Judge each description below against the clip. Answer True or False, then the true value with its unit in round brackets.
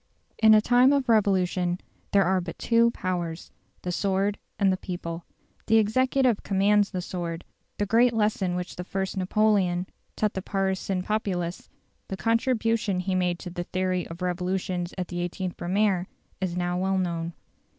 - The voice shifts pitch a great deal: False (2.9 semitones)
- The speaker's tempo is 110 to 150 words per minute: False (160 wpm)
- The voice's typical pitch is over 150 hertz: True (190 Hz)